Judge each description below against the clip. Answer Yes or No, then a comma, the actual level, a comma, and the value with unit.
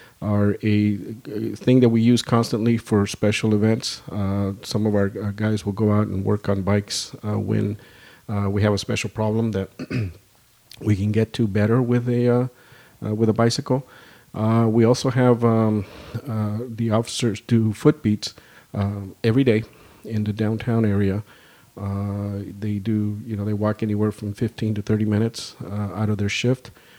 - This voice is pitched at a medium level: No, low, 110 Hz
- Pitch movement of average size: No, narrow, 2.1 semitones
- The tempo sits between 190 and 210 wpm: No, average, 180 wpm